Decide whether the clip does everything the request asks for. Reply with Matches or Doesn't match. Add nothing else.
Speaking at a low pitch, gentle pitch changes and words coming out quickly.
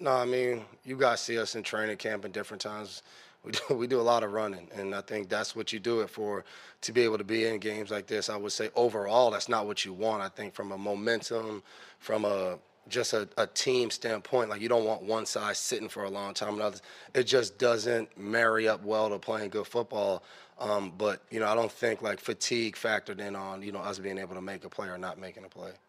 Matches